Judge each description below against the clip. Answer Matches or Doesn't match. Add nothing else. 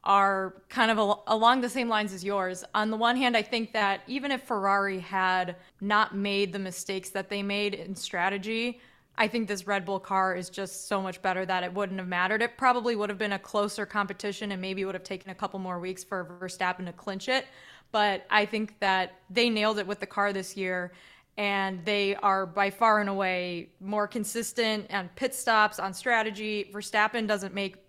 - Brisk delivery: Matches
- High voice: Matches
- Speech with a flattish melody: Matches